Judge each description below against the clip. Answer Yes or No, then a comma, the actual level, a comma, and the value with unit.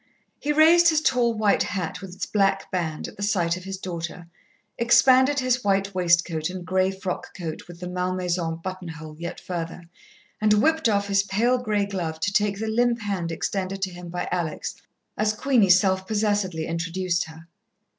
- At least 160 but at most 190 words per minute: Yes, average, 175 wpm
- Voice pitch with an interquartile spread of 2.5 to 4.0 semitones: Yes, average, 3.4 semitones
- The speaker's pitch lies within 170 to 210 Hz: Yes, high, 190 Hz